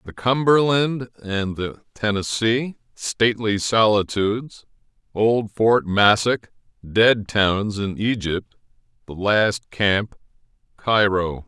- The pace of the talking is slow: Yes, slow, 70 wpm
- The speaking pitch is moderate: No, low, 110 Hz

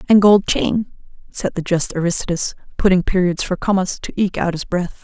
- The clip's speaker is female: Yes, female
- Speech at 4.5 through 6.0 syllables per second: Yes, 5.4 syllables/s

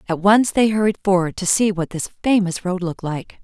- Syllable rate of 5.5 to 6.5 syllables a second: Yes, 5.7 syllables/s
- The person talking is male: No, female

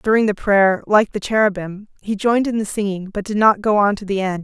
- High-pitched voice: Yes, high, 205 Hz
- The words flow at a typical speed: No, fast, 255 wpm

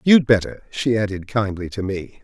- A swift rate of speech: No, average, 190 wpm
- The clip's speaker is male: Yes, male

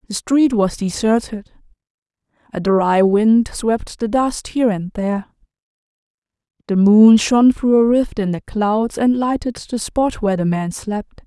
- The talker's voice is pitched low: No, high, 220 Hz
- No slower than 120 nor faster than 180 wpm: Yes, average, 160 wpm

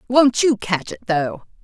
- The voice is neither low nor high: No, high, 195 Hz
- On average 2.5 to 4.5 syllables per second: Yes, 4.1 syllables/s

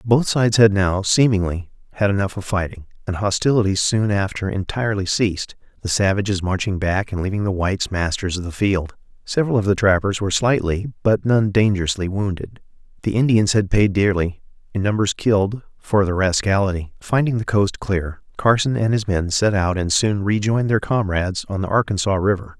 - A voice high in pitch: No, low, 100 Hz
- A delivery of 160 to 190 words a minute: Yes, average, 180 wpm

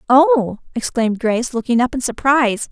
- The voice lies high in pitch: Yes, very high, 250 Hz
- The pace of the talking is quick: No, average, 155 wpm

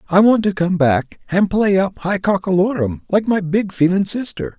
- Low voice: No, medium, 185 Hz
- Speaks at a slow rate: No, average, 195 wpm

